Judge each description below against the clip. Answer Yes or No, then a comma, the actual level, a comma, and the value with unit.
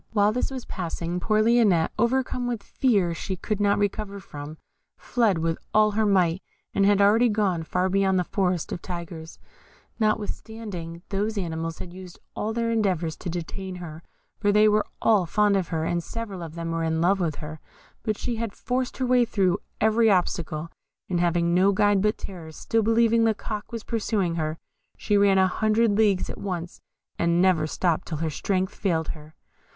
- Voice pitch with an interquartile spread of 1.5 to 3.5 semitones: No, average, 4.1 semitones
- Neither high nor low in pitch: No, high, 195 Hz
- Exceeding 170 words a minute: Yes, average, 190 wpm